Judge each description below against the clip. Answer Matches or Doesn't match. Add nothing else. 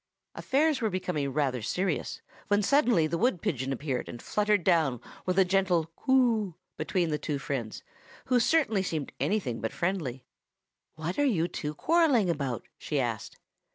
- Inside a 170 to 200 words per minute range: Doesn't match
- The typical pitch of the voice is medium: Matches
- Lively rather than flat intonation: Matches